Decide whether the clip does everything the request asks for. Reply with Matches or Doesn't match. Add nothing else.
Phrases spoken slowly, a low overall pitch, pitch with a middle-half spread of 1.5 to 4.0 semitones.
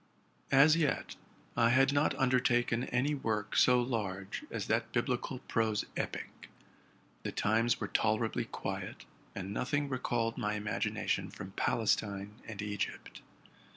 Matches